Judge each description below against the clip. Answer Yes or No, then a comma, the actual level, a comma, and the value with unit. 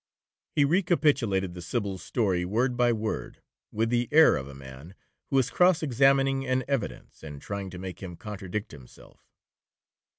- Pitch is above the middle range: No, low, 110 Hz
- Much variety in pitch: Yes, wide, 6.7 semitones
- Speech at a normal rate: Yes, average, 160 wpm